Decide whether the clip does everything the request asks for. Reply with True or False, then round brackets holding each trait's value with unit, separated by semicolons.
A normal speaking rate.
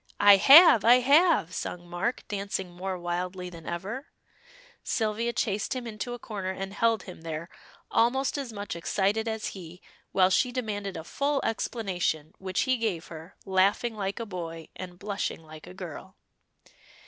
True (160 wpm)